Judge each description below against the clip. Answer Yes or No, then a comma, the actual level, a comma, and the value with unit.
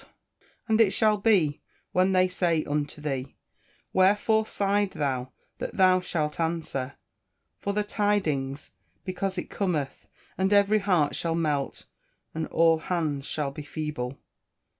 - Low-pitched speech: No, medium, 170 Hz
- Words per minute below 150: Yes, average, 140 wpm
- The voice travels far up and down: No, average, 5.0 semitones